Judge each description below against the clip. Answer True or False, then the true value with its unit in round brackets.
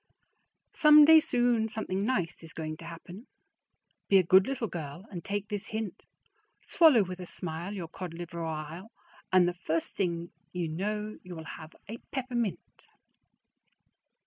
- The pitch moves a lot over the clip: False (4.6 semitones)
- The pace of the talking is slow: False (150 wpm)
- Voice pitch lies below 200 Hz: True (185 Hz)